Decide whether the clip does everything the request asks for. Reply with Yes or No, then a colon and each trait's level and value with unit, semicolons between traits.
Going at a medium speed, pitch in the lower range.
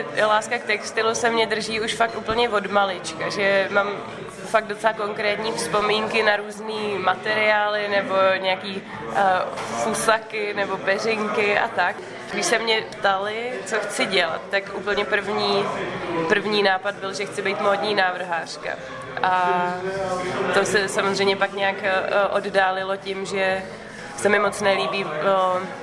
No: average, 140 wpm; high, 200 Hz